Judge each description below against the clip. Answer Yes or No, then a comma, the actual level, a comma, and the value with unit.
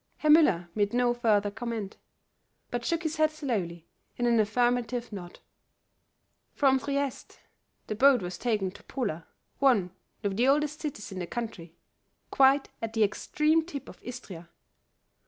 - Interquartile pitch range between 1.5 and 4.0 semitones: No, average, 5.3 semitones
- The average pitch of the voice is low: No, high, 240 Hz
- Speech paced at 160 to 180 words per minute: No, average, 150 wpm